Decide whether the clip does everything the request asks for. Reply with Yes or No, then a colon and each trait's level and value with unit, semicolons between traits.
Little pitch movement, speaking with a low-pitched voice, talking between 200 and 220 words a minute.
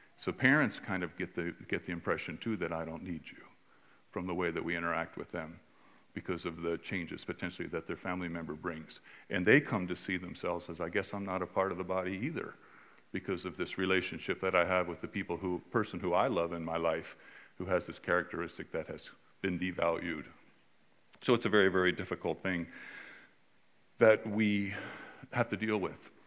Yes: narrow, 2.1 semitones; very low, 90 Hz; fast, 205 wpm